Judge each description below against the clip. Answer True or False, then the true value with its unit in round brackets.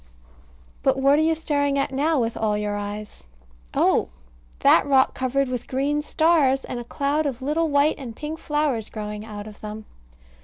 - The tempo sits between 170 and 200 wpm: True (180 wpm)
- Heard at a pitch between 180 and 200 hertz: False (270 Hz)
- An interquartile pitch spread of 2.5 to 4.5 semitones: False (5.2 semitones)